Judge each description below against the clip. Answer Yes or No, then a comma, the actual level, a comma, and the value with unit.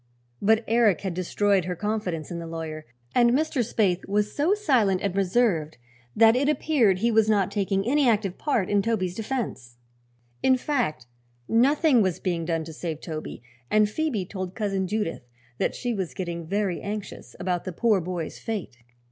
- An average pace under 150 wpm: No, average, 175 wpm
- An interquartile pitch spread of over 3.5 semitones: Yes, average, 4.5 semitones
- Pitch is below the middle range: No, high, 200 Hz